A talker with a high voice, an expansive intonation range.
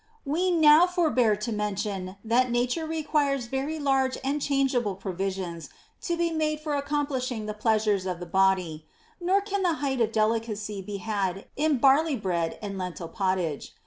Yes: high, 235 Hz; wide, 7.2 semitones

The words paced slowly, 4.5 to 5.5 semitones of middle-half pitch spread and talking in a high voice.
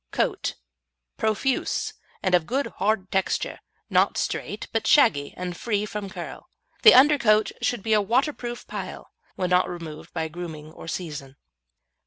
No: average, 145 wpm; average, 5.2 semitones; high, 195 Hz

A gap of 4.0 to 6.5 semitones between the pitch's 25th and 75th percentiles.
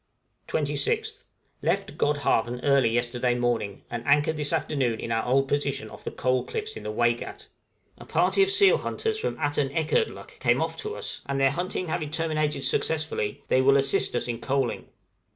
Yes: average, 4.3 semitones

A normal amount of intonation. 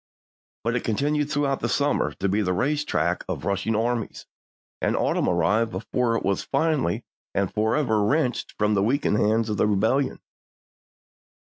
Yes: average, 5.0 semitones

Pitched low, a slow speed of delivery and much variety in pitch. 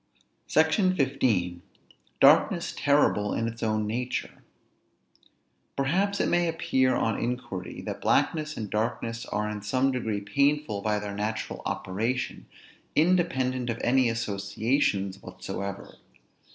No: low, 115 Hz; slow, 115 wpm; average, 4.7 semitones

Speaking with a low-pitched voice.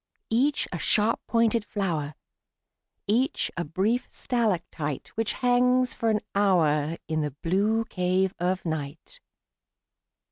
No: high, 195 Hz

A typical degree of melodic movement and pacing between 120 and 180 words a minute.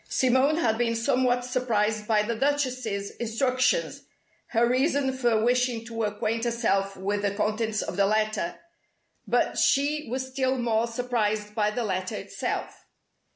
Yes: average, 3.2 semitones; average, 145 wpm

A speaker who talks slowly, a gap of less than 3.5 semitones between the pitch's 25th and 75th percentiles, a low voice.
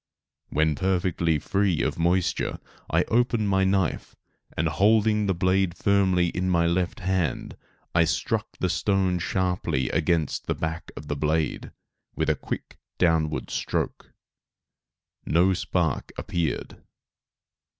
Yes: slow, 125 wpm; average, 2.8 semitones; very low, 90 Hz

